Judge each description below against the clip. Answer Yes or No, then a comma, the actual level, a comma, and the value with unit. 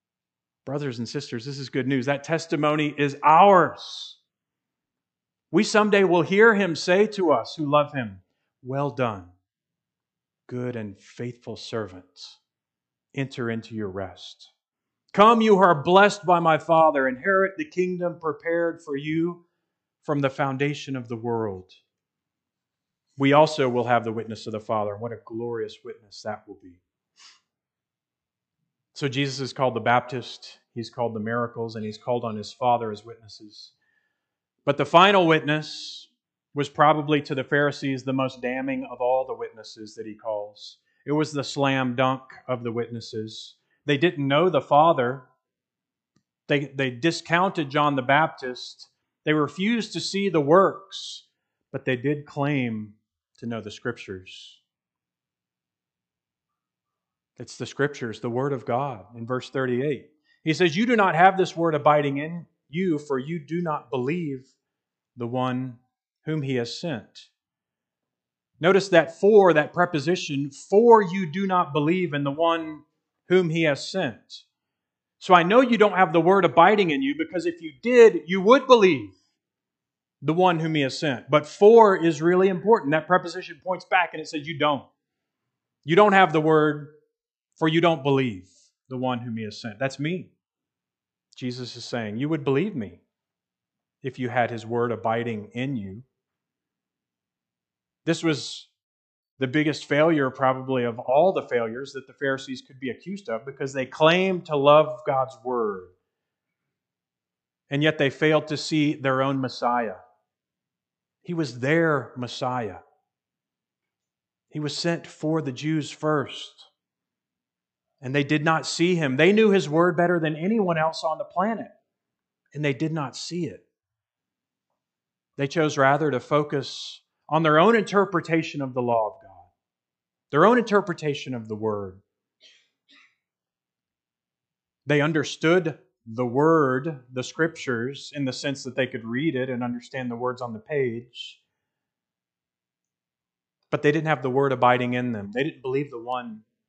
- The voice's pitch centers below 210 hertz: Yes, medium, 140 Hz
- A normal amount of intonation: Yes, average, 5.0 semitones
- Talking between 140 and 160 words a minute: Yes, average, 155 wpm